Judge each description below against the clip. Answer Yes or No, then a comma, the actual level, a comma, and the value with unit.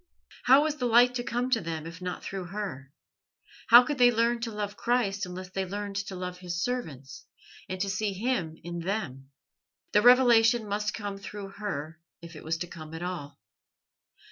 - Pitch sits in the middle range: No, high, 200 Hz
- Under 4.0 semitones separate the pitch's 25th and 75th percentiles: No, average, 5.2 semitones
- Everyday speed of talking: Yes, average, 190 wpm